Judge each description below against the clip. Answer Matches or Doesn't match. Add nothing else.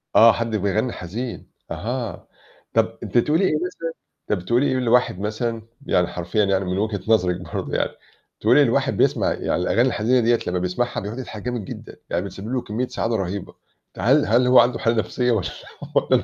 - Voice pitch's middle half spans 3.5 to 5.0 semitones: Matches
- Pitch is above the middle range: Doesn't match